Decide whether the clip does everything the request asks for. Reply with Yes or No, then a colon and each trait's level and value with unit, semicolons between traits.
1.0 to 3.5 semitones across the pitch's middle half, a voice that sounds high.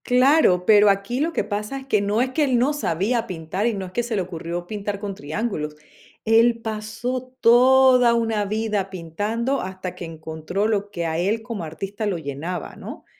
No: average, 4.6 semitones; high, 210 Hz